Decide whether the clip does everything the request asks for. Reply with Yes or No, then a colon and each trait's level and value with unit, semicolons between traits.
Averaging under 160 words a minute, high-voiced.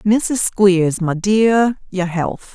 Yes: average, 140 wpm; high, 195 Hz